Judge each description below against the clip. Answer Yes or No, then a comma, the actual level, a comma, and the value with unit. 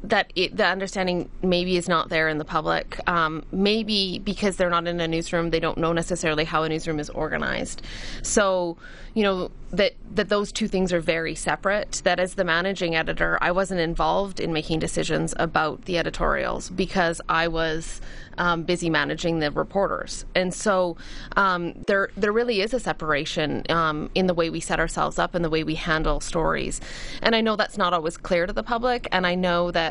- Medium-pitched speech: Yes, medium, 175 Hz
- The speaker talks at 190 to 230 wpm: Yes, average, 195 wpm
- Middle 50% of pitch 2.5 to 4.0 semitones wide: Yes, average, 3.1 semitones